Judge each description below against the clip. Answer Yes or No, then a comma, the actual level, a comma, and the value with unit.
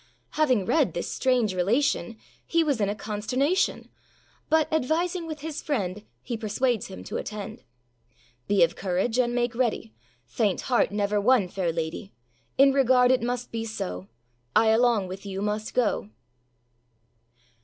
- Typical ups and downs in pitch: Yes, average, 4.4 semitones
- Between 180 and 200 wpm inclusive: No, average, 150 wpm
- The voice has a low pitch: No, high, 225 Hz